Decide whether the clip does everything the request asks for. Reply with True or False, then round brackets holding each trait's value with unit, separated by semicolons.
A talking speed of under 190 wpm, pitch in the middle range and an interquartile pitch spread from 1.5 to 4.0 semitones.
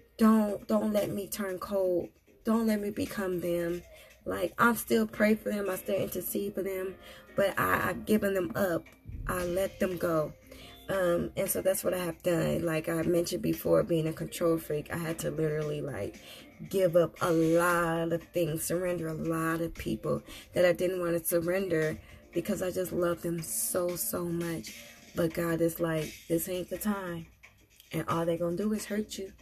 False (195 wpm; 175 Hz; 2.5 semitones)